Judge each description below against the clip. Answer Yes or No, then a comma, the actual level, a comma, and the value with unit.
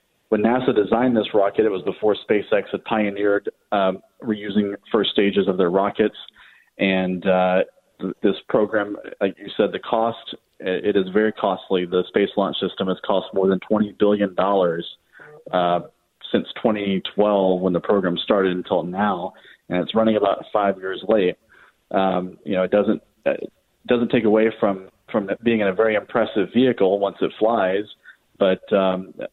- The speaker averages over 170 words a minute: No, average, 165 wpm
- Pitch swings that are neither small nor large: No, narrow, 2.3 semitones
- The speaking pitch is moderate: No, low, 100 Hz